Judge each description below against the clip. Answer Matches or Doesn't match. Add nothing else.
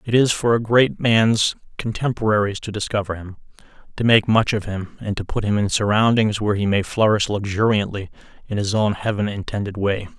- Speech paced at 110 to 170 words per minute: Doesn't match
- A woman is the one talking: Doesn't match